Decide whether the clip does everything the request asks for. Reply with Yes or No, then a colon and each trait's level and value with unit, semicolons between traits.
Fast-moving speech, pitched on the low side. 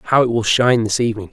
Yes: fast, 275 wpm; low, 115 Hz